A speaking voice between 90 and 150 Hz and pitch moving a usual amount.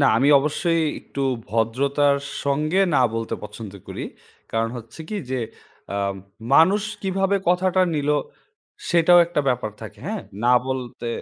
No: medium, 140 Hz; wide, 7.3 semitones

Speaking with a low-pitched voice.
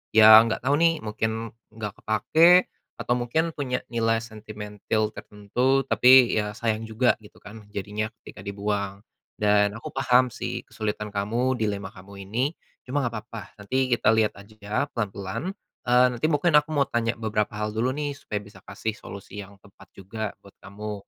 Yes: low, 110 Hz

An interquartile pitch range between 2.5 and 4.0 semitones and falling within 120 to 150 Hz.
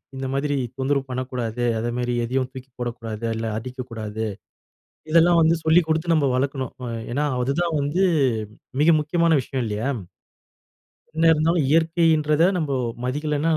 No: average, 4.4 semitones; medium, 140 Hz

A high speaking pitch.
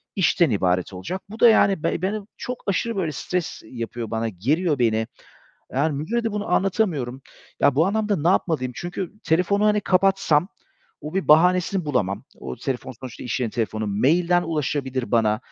No: medium, 155 Hz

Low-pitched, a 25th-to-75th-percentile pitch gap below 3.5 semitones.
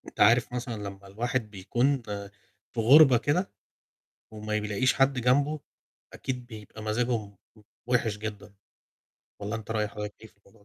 Yes: low, 110 Hz; average, 3.1 semitones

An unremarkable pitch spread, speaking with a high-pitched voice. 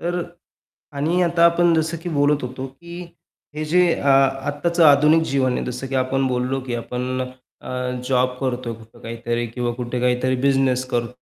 No: average, 3.1 semitones; low, 130 Hz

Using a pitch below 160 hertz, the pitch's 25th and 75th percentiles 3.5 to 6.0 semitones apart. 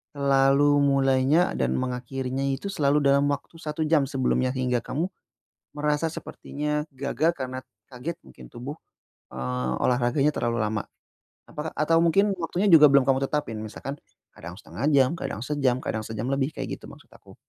No: medium, 140 Hz; average, 2.9 semitones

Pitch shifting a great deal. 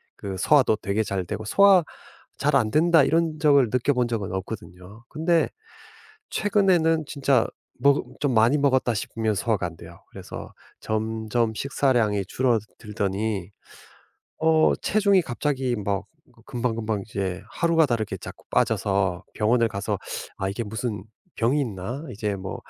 Yes: wide, 5.7 semitones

